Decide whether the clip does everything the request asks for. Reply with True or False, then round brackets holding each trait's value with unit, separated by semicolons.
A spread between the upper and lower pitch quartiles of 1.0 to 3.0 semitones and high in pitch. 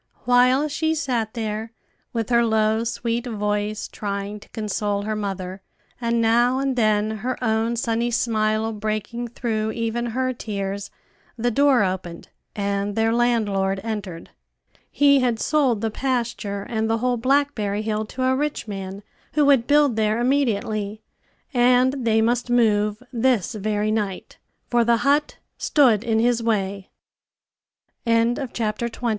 True (2.6 semitones; 225 Hz)